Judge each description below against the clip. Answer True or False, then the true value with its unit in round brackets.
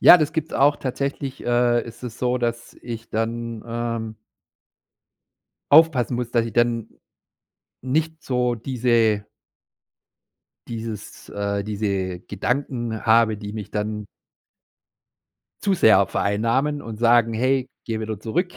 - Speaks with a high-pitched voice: False (115 Hz)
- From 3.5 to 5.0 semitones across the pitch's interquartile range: False (2.6 semitones)